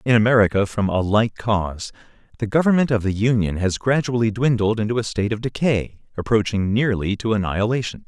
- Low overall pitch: Yes, low, 110 Hz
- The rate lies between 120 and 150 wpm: No, average, 170 wpm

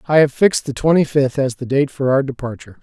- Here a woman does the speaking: No, male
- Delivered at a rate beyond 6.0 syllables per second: Yes, 6.4 syllables/s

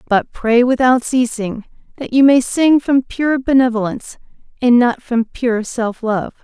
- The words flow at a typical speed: Yes, average, 160 wpm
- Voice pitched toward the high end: Yes, high, 245 Hz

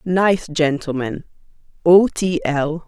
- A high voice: No, medium, 165 Hz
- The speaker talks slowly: Yes, slow, 85 wpm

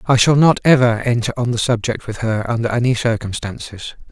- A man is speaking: Yes, male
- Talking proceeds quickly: No, average, 190 wpm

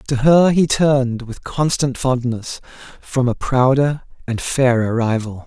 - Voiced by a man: Yes, male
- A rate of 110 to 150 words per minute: Yes, average, 145 wpm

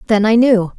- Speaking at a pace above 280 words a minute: No, fast, 230 wpm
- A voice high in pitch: Yes, high, 215 Hz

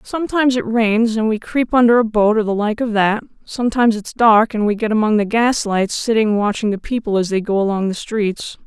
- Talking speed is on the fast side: Yes, fast, 230 wpm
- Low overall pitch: No, high, 220 Hz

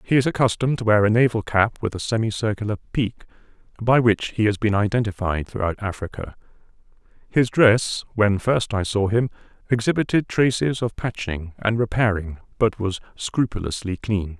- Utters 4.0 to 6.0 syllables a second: Yes, 5.2 syllables/s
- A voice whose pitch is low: Yes, low, 110 Hz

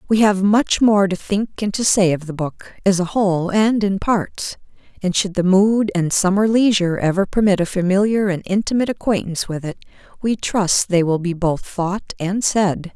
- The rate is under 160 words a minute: No, average, 200 wpm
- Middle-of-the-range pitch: No, high, 195 Hz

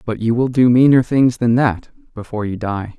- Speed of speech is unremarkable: No, fast, 220 wpm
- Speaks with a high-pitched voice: No, low, 115 Hz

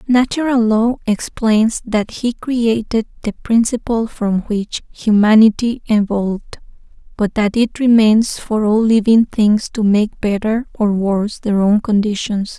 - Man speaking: No, female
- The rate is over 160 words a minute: No, slow, 135 wpm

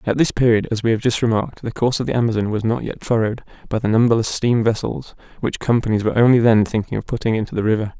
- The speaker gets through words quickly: Yes, fast, 250 wpm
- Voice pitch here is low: Yes, low, 115 Hz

